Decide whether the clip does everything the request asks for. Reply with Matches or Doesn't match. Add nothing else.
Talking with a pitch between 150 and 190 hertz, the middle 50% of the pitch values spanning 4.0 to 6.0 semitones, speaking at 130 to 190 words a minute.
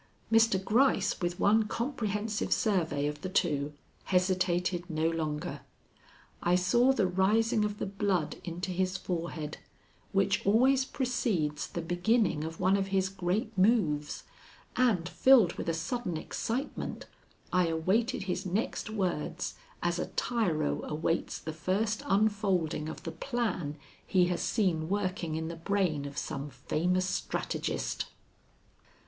Matches